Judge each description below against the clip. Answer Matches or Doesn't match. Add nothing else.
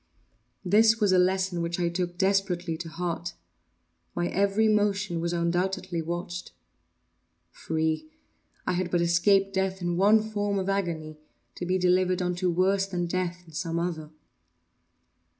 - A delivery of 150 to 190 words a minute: Doesn't match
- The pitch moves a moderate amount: Doesn't match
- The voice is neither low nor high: Matches